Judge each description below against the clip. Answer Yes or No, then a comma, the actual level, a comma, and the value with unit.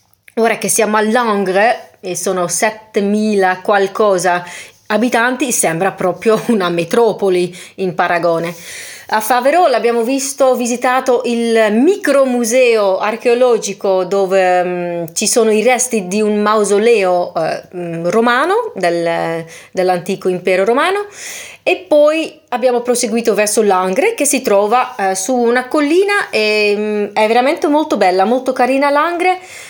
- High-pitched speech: Yes, high, 220 Hz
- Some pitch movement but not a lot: Yes, average, 4.9 semitones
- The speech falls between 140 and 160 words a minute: No, average, 125 wpm